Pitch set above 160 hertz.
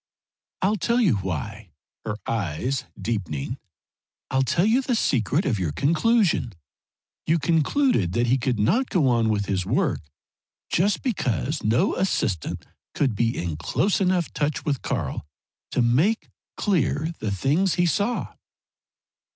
No: low, 135 Hz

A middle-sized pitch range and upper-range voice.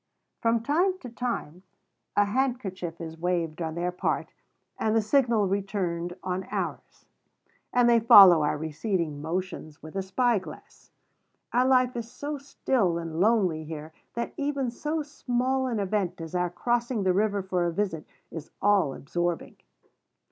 No: wide, 6.0 semitones; high, 195 Hz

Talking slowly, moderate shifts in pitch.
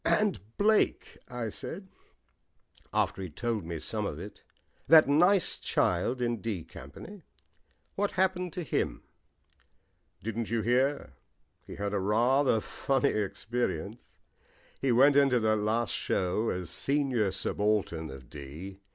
No: slow, 130 wpm; wide, 6.0 semitones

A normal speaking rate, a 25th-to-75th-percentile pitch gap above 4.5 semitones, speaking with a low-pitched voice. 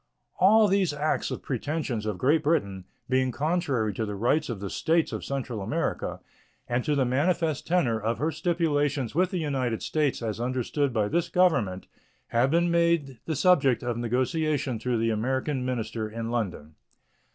Yes: average, 170 wpm; wide, 5.4 semitones; low, 130 Hz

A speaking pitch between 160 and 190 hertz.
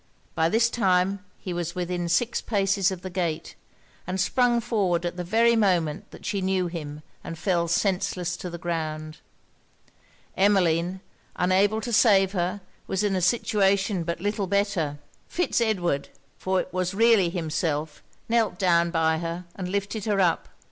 Yes: medium, 185 Hz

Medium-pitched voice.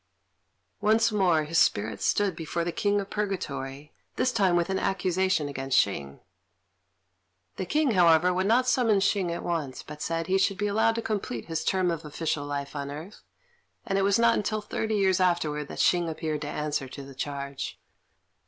Yes: medium, 175 Hz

